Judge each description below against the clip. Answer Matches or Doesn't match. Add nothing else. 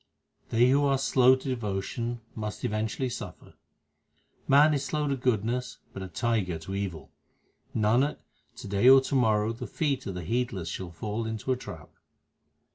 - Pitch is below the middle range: Matches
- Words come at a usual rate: Matches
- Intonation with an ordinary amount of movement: Matches